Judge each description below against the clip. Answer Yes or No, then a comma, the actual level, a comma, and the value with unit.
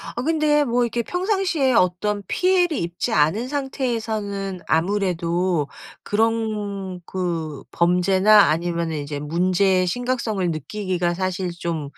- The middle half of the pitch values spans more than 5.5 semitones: No, average, 5.2 semitones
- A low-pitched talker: No, high, 190 Hz